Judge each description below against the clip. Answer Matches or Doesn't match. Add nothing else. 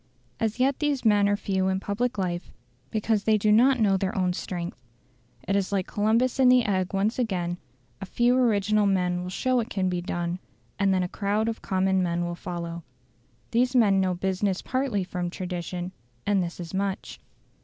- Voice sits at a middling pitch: Doesn't match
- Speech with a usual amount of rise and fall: Matches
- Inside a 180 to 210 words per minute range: Matches